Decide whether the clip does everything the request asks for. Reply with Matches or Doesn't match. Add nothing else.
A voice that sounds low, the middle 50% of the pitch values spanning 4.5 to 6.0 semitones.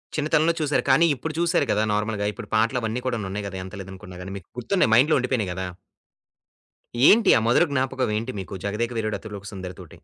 Matches